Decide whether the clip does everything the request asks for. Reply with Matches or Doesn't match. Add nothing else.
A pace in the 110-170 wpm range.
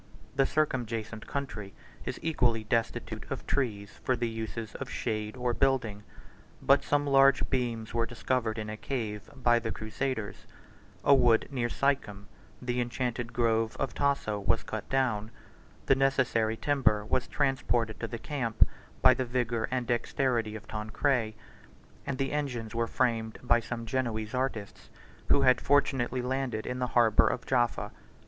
Matches